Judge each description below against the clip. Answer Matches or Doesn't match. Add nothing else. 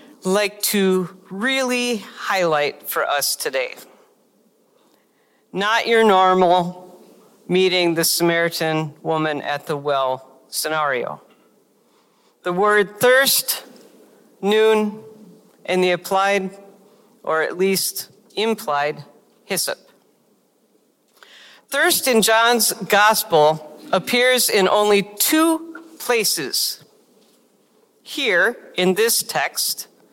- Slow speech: Matches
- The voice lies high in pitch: Matches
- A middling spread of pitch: Matches